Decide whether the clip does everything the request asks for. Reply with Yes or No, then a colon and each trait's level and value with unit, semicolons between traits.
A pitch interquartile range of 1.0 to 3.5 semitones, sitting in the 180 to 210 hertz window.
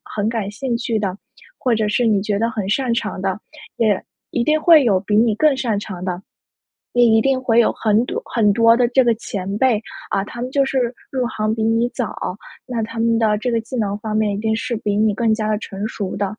No: narrow, 2.4 semitones; high, 225 Hz